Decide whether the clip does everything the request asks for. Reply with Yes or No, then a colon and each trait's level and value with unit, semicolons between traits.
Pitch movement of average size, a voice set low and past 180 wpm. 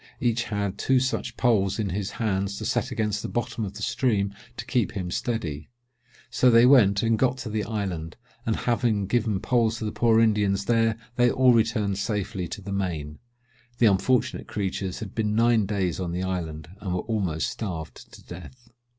Yes: average, 3.4 semitones; low, 105 Hz; average, 190 wpm